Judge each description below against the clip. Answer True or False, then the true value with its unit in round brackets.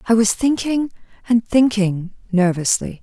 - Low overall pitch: False (220 Hz)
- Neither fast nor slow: False (100 wpm)